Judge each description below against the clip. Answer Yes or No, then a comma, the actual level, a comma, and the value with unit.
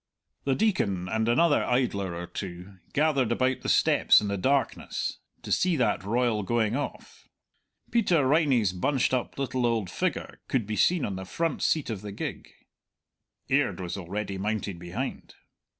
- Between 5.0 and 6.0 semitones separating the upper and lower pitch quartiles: Yes, wide, 5.5 semitones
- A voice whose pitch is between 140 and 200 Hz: No, low, 115 Hz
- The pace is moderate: Yes, average, 160 wpm